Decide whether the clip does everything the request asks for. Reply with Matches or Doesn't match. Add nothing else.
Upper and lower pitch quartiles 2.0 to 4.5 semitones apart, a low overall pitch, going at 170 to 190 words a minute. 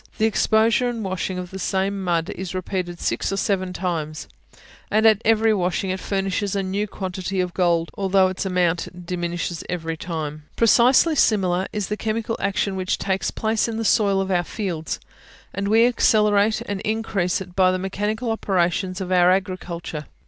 Doesn't match